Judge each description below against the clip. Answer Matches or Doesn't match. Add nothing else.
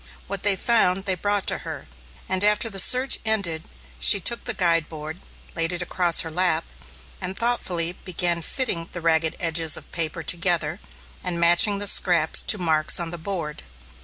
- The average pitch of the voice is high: Doesn't match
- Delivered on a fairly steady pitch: Doesn't match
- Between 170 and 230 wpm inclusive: Matches